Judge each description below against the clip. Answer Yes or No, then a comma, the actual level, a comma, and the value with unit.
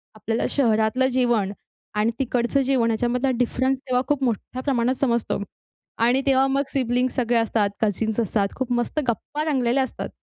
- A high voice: Yes, high, 245 Hz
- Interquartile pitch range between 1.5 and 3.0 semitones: Yes, narrow, 2.4 semitones